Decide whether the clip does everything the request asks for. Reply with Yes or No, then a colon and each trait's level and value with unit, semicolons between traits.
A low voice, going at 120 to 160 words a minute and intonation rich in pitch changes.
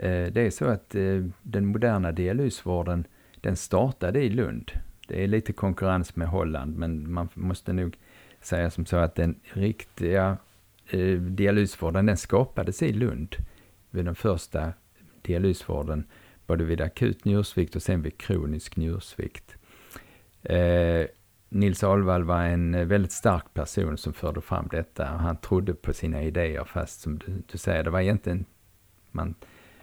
No: very low, 90 Hz; average, 140 wpm; average, 2.9 semitones